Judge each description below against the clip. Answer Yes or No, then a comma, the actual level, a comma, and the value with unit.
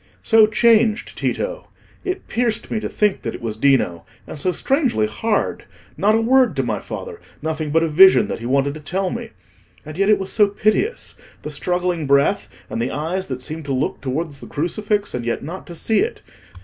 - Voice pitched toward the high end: No, medium, 180 Hz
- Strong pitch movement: Yes, wide, 7.3 semitones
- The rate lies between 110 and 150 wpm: No, average, 200 wpm